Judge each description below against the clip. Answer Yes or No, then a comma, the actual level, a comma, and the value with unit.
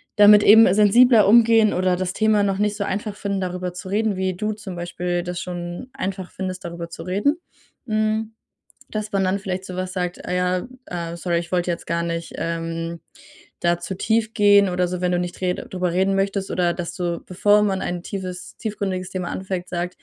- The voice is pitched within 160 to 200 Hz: Yes, medium, 185 Hz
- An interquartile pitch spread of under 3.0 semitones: Yes, narrow, 2.6 semitones